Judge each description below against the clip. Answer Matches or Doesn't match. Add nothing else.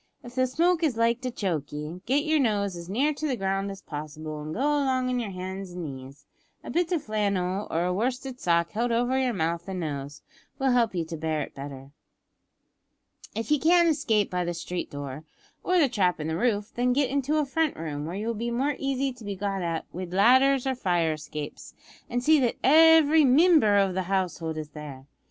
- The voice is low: Doesn't match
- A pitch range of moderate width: Doesn't match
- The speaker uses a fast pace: Matches